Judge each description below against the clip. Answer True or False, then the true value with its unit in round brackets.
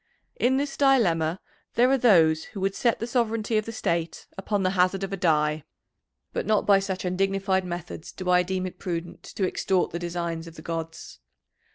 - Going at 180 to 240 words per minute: True (195 wpm)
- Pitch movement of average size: True (3.5 semitones)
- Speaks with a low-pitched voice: False (185 Hz)